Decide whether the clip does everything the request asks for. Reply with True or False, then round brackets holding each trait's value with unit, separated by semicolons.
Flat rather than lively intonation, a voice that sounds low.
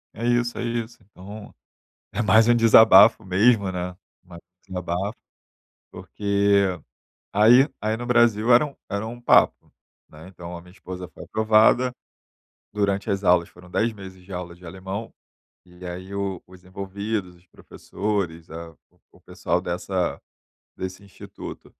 False (3.4 semitones; 100 Hz)